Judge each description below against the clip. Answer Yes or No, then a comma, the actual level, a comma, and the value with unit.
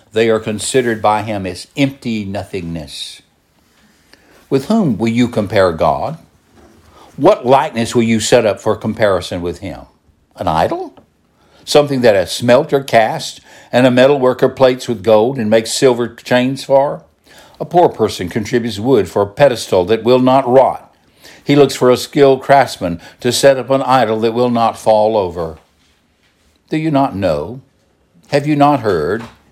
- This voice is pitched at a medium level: No, low, 115 Hz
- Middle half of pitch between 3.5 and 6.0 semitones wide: Yes, average, 4.2 semitones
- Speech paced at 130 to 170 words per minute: Yes, average, 165 wpm